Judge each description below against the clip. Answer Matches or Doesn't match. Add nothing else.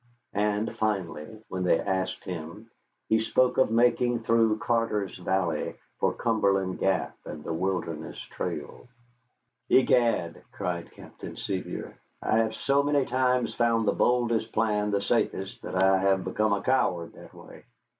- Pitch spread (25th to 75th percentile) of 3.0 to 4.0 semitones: Matches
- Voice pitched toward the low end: Matches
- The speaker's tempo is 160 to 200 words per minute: Doesn't match